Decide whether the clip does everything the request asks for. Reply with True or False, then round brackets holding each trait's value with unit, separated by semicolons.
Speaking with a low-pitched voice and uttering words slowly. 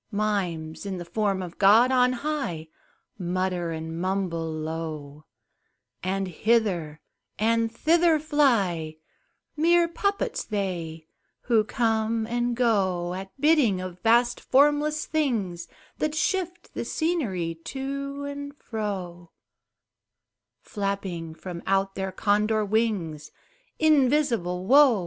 False (210 Hz; 110 wpm)